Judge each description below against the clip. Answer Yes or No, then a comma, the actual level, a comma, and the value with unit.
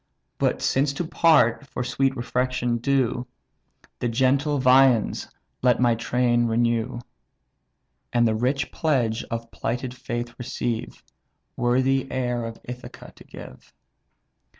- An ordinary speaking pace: No, slow, 125 wpm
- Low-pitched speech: Yes, low, 125 Hz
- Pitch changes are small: Yes, narrow, 1.9 semitones